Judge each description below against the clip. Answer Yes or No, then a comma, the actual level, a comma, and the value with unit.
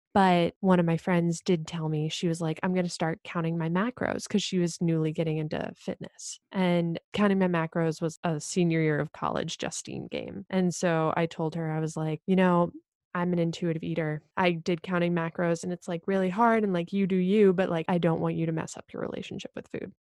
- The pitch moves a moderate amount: No, narrow, 2.2 semitones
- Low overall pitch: No, medium, 170 Hz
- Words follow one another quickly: Yes, fast, 230 wpm